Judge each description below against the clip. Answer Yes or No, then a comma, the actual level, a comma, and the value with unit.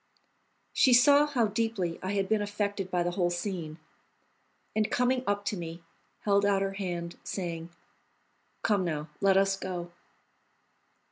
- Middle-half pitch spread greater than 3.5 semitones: No, average, 3.0 semitones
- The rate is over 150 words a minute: No, average, 145 wpm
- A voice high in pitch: Yes, high, 195 Hz